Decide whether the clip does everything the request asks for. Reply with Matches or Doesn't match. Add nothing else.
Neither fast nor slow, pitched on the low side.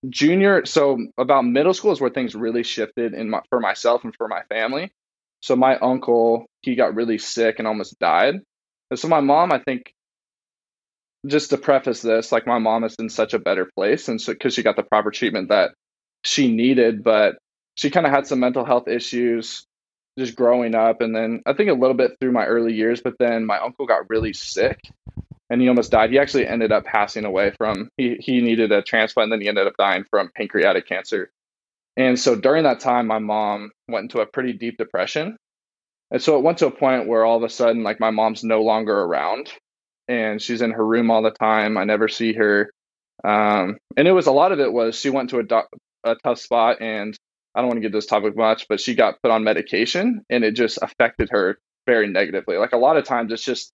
Doesn't match